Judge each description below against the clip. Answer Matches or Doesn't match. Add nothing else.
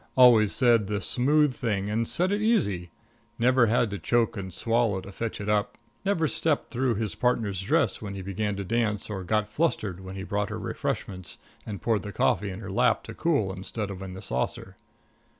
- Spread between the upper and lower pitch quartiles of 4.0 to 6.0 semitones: Doesn't match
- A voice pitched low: Matches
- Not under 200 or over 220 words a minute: Matches